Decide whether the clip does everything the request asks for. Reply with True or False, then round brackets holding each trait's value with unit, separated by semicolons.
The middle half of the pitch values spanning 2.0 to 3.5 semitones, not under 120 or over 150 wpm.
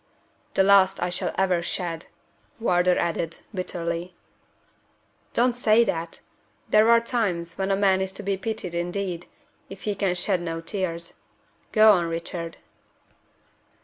True (2.7 semitones; 140 wpm)